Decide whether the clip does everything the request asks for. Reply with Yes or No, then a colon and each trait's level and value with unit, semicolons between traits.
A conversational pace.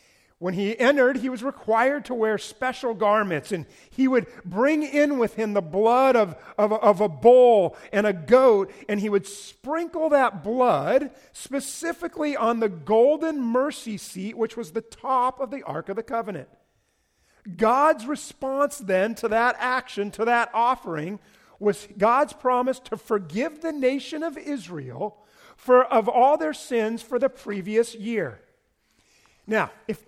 Yes: average, 155 wpm